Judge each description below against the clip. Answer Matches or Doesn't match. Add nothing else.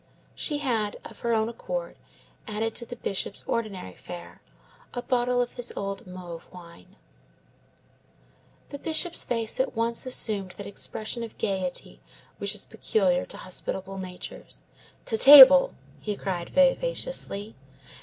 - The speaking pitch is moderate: Doesn't match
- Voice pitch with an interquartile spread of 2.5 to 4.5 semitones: Doesn't match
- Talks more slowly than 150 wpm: Matches